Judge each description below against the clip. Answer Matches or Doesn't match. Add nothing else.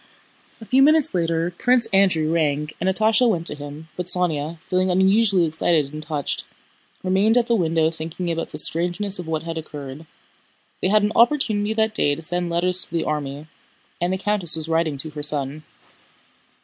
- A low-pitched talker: Doesn't match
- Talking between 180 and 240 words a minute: Matches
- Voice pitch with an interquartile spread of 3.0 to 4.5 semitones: Matches